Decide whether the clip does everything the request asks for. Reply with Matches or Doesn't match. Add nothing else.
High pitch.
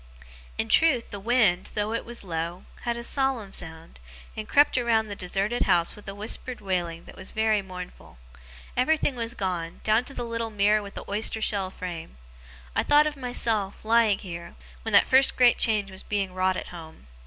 Matches